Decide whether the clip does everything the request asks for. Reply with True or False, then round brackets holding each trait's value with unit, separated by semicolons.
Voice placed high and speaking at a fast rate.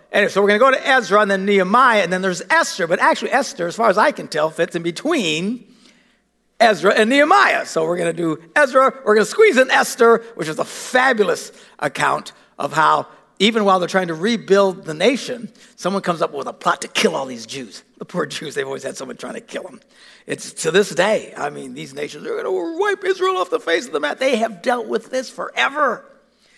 True (230 Hz; 235 wpm)